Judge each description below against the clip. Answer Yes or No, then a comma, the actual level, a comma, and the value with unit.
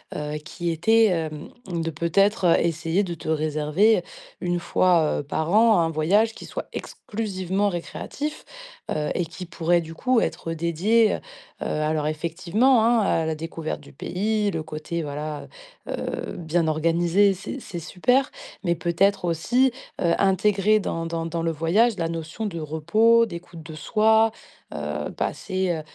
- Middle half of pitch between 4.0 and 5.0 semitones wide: Yes, average, 4.3 semitones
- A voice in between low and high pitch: Yes, medium, 170 Hz